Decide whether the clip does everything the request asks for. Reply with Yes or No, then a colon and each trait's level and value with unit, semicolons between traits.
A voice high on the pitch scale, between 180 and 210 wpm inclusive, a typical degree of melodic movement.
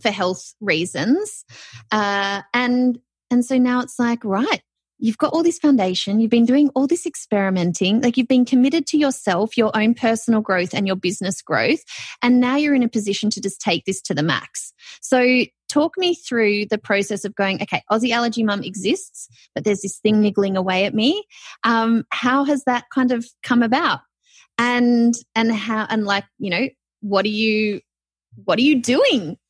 Yes: high, 230 Hz; average, 185 wpm; average, 4.2 semitones